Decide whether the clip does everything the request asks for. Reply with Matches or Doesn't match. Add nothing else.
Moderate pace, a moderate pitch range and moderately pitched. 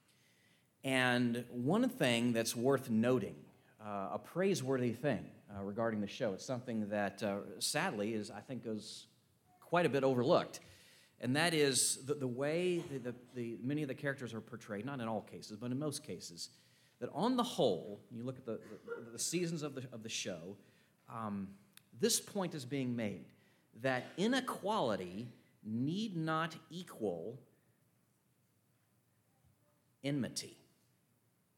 Doesn't match